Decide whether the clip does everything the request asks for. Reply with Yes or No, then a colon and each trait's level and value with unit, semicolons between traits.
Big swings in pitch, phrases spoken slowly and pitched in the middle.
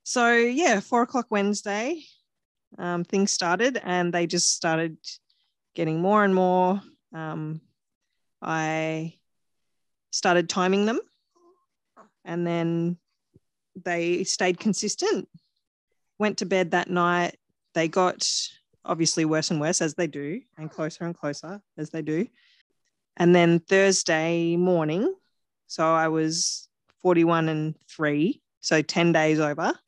No: average, 3.8 semitones; slow, 120 wpm; medium, 175 Hz